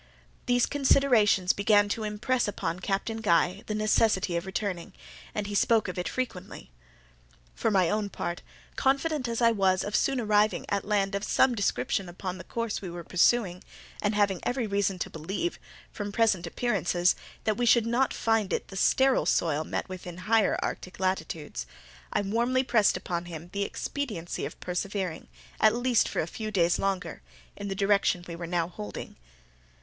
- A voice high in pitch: Yes, high, 200 Hz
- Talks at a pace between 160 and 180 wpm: Yes, average, 175 wpm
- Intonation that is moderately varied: Yes, average, 3.8 semitones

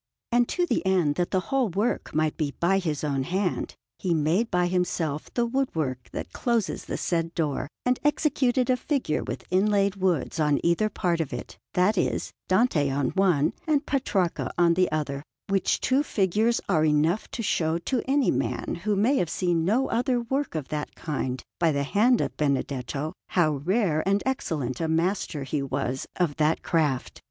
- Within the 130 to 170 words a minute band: No, average, 185 wpm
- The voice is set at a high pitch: No, medium, 175 Hz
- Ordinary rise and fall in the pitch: No, wide, 6.2 semitones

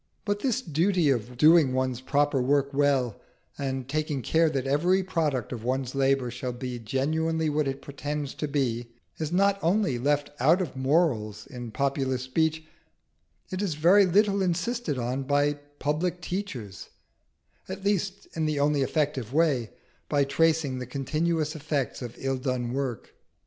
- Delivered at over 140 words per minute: Yes, average, 155 wpm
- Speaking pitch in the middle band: Yes, medium, 145 Hz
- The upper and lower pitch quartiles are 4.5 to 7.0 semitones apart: No, average, 3.9 semitones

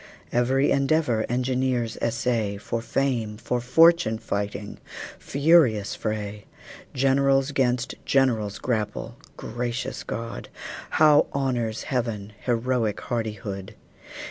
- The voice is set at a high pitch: No, low, 120 Hz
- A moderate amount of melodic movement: Yes, average, 3.4 semitones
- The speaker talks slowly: Yes, slow, 90 wpm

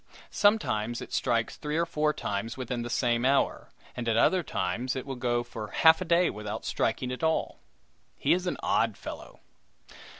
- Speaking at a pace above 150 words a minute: Yes, average, 190 wpm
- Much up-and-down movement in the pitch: Yes, wide, 5.7 semitones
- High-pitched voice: No, low, 125 Hz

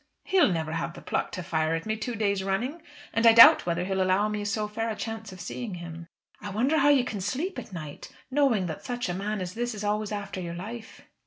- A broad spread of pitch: No, average, 4.0 semitones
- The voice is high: Yes, high, 205 Hz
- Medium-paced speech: No, fast, 245 wpm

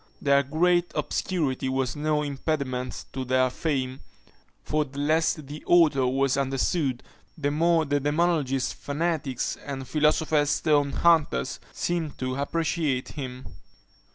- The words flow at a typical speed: No, slow, 125 wpm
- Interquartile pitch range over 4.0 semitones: No, average, 3.0 semitones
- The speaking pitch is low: No, medium, 145 Hz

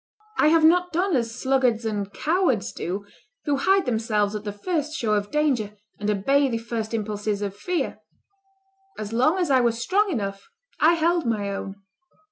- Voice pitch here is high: Yes, high, 235 Hz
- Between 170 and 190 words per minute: Yes, average, 175 wpm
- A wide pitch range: Yes, wide, 7.0 semitones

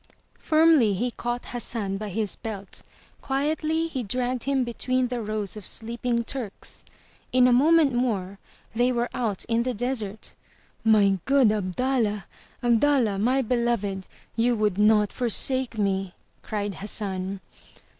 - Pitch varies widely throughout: No, average, 3.5 semitones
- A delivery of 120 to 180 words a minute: Yes, slow, 135 wpm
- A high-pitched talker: Yes, high, 235 Hz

